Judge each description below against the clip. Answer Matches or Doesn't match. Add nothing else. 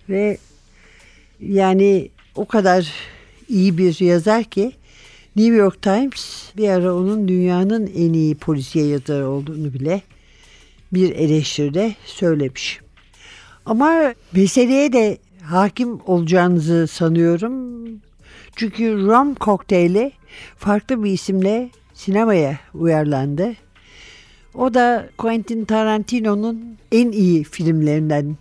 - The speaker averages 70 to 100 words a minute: Matches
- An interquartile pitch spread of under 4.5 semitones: Doesn't match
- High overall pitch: Matches